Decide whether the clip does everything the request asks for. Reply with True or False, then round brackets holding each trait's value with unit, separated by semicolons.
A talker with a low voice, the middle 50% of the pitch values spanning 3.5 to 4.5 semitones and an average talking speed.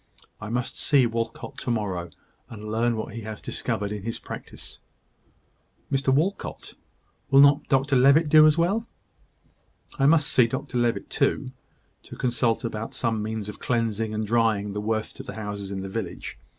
True (115 Hz; 4.1 semitones; 170 wpm)